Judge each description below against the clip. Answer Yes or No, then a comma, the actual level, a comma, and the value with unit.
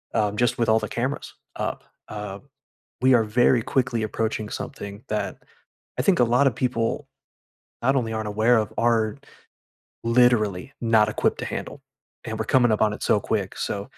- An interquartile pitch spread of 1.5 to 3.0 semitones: Yes, narrow, 2.4 semitones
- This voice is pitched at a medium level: No, low, 115 Hz